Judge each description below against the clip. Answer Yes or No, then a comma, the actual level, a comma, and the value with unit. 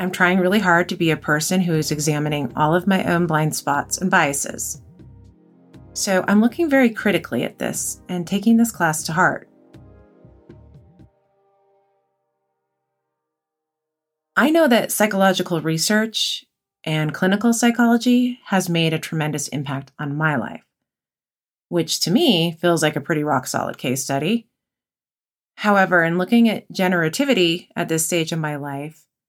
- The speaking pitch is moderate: Yes, medium, 170 Hz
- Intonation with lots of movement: No, average, 4.5 semitones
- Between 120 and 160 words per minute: Yes, average, 145 wpm